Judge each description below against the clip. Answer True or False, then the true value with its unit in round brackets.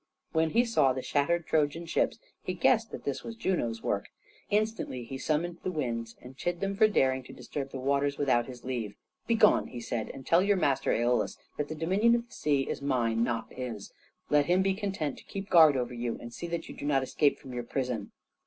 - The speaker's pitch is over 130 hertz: True (140 Hz)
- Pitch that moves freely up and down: True (5.8 semitones)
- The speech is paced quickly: True (220 wpm)